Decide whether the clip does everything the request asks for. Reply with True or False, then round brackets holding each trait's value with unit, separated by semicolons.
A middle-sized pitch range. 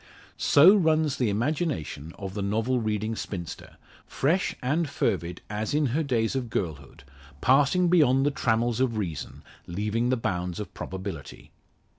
False (6.3 semitones)